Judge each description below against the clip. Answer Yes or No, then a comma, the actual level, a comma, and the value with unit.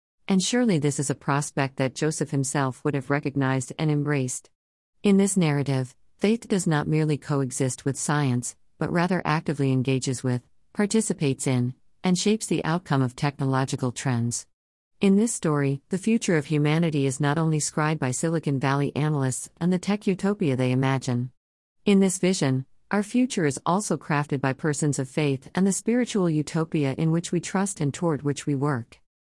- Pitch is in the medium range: Yes, medium, 150 Hz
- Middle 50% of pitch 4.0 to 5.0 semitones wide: Yes, average, 4.5 semitones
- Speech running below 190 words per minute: Yes, average, 175 wpm